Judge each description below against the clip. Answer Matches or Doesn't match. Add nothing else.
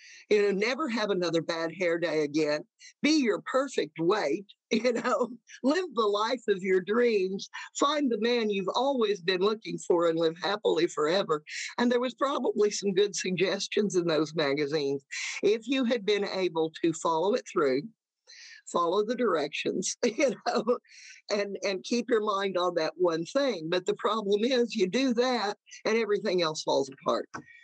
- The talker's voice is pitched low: Doesn't match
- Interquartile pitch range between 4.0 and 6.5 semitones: Matches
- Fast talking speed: Doesn't match